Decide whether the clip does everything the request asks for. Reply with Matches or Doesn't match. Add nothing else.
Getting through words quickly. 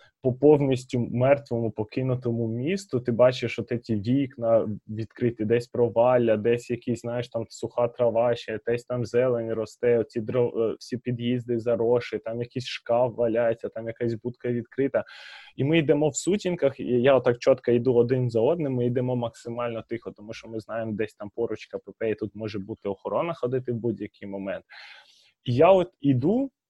Matches